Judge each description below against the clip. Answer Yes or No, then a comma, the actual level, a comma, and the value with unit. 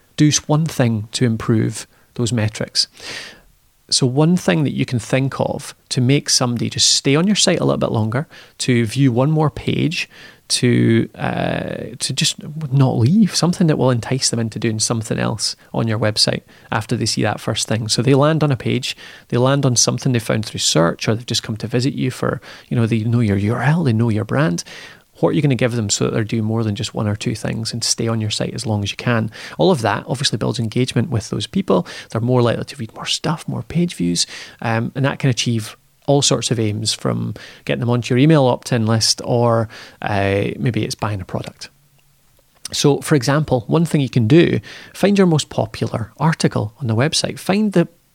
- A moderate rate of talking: No, fast, 220 wpm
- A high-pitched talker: No, low, 125 Hz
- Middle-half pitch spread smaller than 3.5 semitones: No, average, 4.0 semitones